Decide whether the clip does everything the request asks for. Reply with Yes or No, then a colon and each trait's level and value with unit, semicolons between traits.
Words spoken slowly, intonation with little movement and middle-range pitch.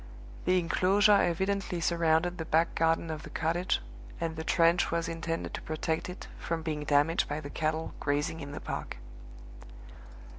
No: average, 160 wpm; narrow, 1.6 semitones; medium, 165 Hz